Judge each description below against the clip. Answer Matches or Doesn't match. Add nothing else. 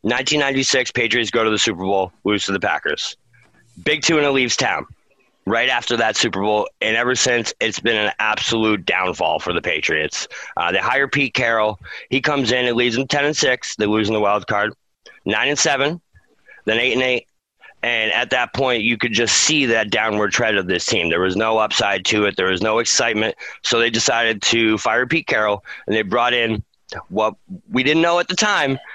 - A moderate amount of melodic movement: Matches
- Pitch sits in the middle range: Doesn't match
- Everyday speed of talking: Doesn't match